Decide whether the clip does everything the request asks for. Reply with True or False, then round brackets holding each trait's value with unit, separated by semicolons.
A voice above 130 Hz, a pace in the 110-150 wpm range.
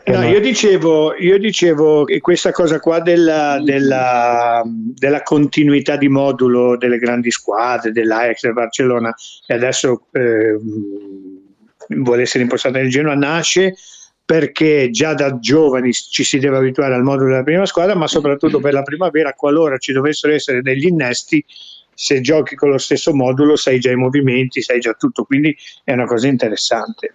False (140 Hz; 160 wpm)